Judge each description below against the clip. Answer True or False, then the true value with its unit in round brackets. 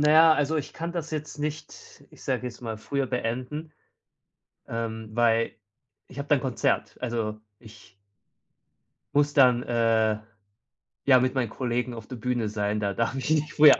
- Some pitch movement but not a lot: True (4.4 semitones)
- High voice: False (125 Hz)